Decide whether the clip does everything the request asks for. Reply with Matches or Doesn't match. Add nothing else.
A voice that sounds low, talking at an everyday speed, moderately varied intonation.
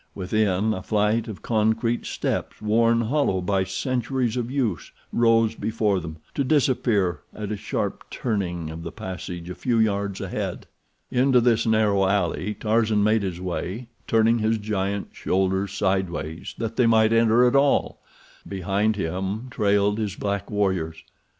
Matches